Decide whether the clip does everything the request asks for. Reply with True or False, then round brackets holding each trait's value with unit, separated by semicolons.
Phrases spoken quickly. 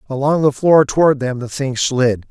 True (210 wpm)